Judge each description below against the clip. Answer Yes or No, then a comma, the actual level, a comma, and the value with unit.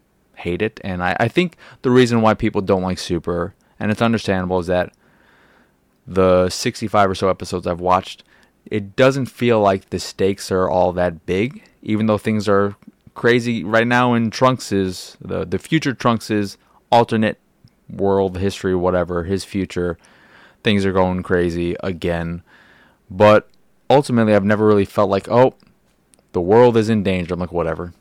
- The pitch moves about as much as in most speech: Yes, average, 3.6 semitones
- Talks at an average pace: Yes, average, 165 wpm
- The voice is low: Yes, low, 100 Hz